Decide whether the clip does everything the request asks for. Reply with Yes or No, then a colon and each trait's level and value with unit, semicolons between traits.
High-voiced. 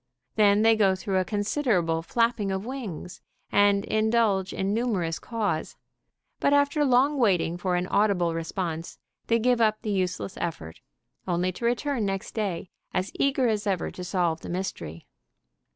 Yes: high, 200 Hz